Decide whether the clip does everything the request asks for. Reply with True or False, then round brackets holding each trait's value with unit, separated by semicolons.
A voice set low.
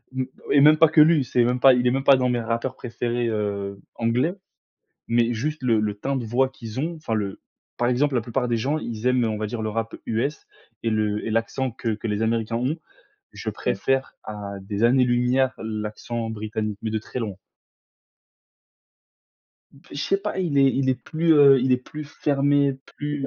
True (120 Hz)